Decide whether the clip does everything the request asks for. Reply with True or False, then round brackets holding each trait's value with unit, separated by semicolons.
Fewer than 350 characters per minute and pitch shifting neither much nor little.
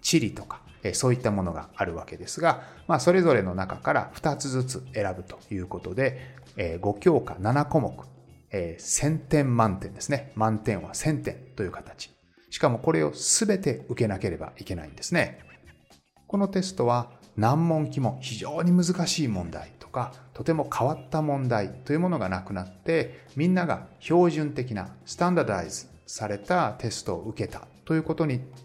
False (320 characters per minute; 8.0 semitones)